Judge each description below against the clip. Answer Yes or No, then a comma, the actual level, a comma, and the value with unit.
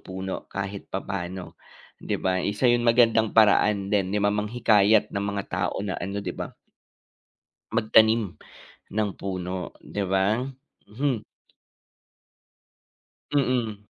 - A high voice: No, low, 105 Hz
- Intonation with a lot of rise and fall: No, narrow, 2.5 semitones